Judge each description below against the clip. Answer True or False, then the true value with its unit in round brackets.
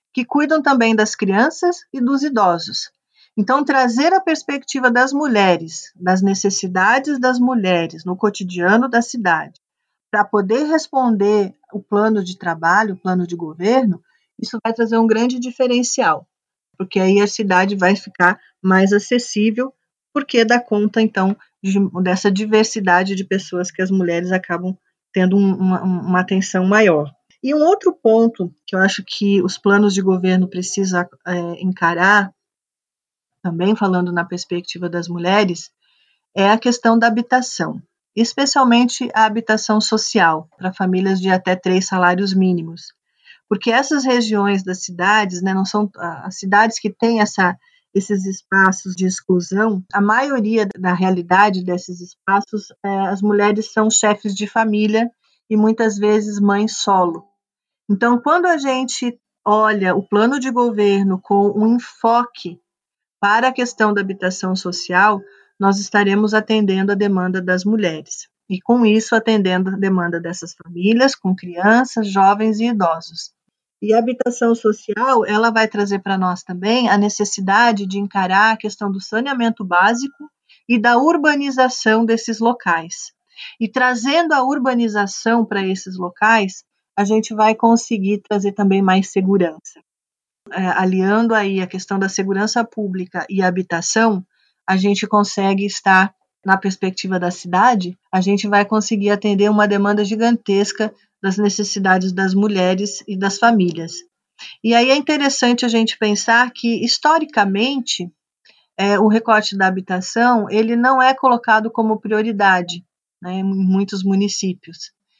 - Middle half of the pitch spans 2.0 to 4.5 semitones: True (3.4 semitones)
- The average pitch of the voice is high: True (205 Hz)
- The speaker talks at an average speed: True (140 wpm)